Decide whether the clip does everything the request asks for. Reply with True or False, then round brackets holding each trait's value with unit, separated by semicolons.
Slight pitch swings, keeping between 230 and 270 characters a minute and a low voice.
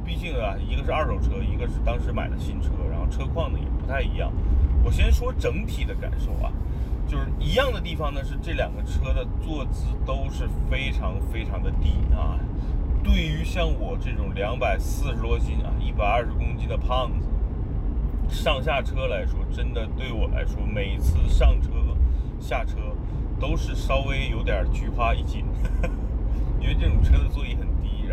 True (2.0 semitones; 260 characters per minute; 75 Hz)